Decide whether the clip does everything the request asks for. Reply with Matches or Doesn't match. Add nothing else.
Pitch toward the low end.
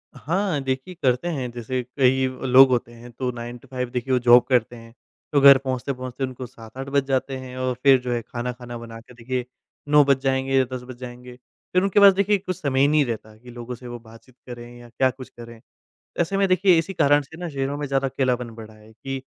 Matches